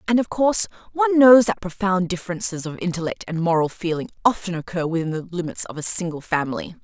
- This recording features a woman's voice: Yes, female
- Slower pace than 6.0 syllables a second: No, 6.4 syllables/s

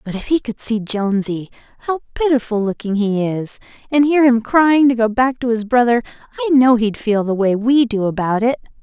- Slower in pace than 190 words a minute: No, fast, 205 wpm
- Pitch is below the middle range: No, high, 235 Hz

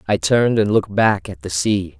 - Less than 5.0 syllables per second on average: No, 5.5 syllables/s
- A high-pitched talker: No, low, 100 Hz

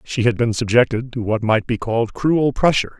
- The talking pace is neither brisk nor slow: No, fast, 220 wpm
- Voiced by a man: Yes, male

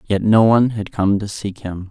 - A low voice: Yes, low, 105 Hz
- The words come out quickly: Yes, fast, 250 wpm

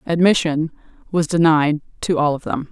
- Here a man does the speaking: No, female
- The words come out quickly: No, average, 155 wpm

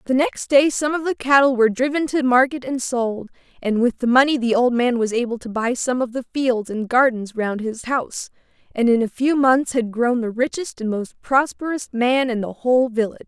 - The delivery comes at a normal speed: No, fast, 225 wpm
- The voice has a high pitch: Yes, very high, 250 Hz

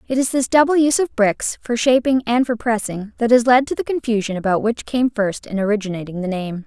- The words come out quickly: Yes, fast, 235 wpm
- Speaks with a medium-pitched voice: No, high, 230 Hz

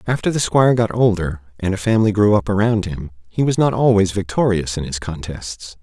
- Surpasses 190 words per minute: Yes, fast, 205 wpm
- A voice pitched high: No, low, 100 Hz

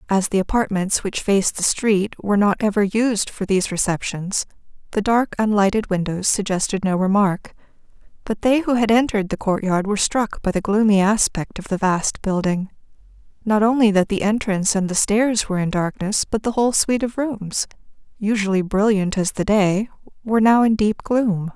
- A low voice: No, high, 205 Hz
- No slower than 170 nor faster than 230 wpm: Yes, average, 180 wpm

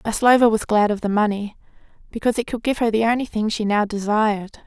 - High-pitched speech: Yes, high, 220 Hz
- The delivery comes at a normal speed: No, fast, 220 wpm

